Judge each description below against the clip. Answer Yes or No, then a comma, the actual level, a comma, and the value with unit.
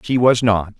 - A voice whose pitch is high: No, low, 110 Hz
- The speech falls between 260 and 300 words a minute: No, fast, 225 wpm